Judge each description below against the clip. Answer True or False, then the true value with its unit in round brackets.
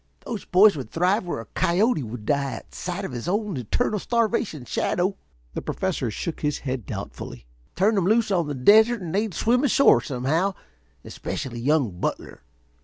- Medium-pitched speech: True (175 Hz)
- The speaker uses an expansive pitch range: True (7.7 semitones)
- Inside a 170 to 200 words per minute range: True (175 wpm)